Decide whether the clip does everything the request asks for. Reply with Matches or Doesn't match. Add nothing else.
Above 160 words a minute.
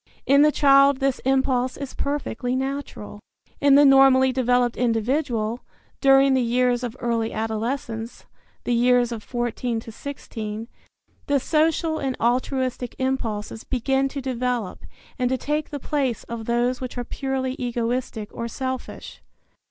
Doesn't match